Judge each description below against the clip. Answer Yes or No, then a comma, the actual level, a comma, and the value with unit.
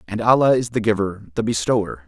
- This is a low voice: Yes, low, 110 Hz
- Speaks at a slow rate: No, fast, 205 wpm